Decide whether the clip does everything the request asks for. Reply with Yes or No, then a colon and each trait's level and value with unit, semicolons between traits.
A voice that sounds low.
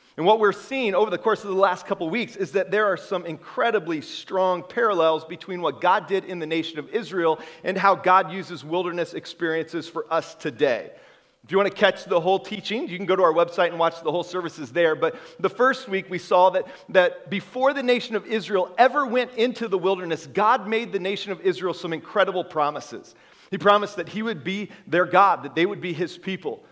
No: medium, 185 Hz